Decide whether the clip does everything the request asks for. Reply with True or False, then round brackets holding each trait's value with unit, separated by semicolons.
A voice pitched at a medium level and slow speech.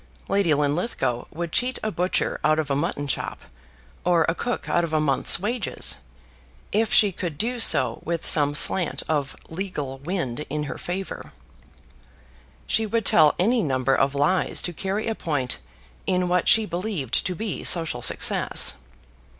False (170 Hz; 160 wpm)